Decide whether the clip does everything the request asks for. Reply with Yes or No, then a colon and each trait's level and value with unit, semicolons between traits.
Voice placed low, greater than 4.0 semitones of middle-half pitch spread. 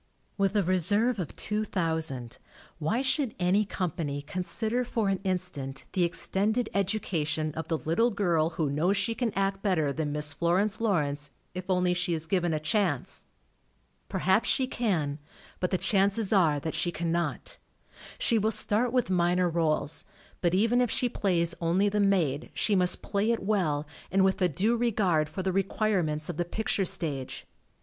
No: medium, 185 Hz; average, 4.4 semitones